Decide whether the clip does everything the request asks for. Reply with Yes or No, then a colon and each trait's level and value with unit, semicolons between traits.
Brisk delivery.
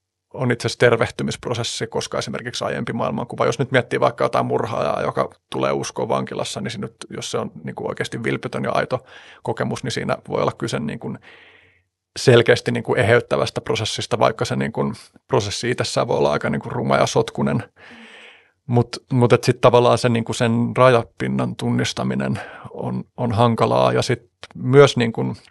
Yes: fast, 160 wpm